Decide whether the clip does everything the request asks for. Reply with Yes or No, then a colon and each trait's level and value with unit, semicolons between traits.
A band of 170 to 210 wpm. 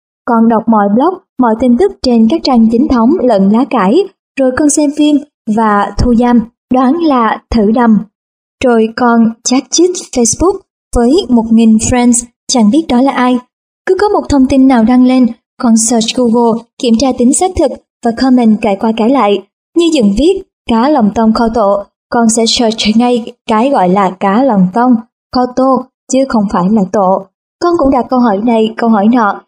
Yes: average, 195 wpm